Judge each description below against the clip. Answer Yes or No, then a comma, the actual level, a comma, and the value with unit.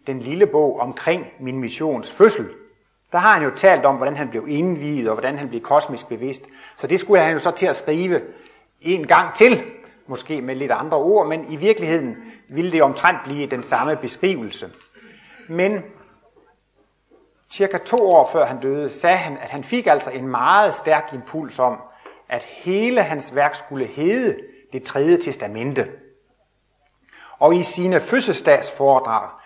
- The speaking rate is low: No, average, 165 wpm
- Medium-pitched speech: Yes, medium, 155 Hz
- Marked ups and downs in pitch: Yes, wide, 7.2 semitones